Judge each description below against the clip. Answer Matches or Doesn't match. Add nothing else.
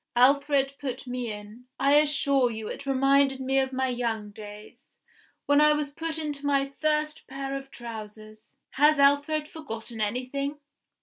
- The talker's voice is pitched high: Matches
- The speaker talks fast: Doesn't match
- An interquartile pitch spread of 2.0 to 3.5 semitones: Matches